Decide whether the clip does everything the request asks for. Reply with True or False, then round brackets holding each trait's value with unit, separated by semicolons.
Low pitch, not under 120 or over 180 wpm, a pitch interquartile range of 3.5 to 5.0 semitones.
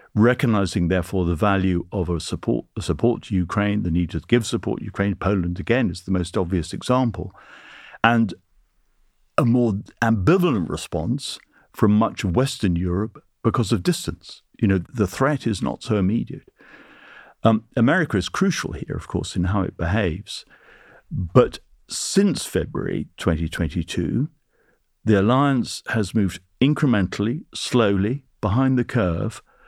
True (105 Hz; 140 wpm; 4.7 semitones)